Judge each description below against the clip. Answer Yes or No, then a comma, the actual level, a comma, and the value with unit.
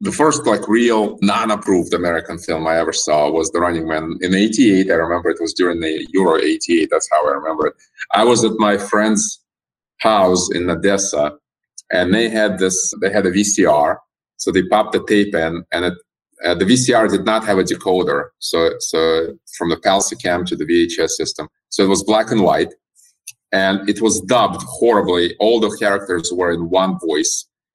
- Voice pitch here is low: Yes, low, 100 Hz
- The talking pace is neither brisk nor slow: Yes, average, 190 wpm